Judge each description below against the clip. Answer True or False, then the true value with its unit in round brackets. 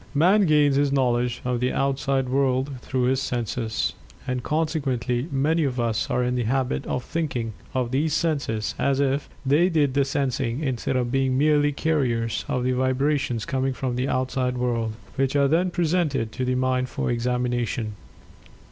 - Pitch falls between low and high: False (130 Hz)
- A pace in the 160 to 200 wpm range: True (170 wpm)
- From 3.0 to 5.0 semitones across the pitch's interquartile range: False (2.4 semitones)